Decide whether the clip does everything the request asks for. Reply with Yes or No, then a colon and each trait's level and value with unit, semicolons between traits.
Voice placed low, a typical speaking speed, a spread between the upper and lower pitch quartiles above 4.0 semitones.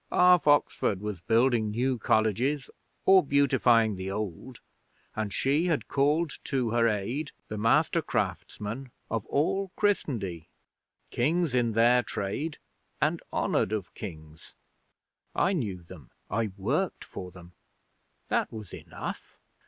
No: low, 115 Hz; slow, 125 wpm; wide, 5.5 semitones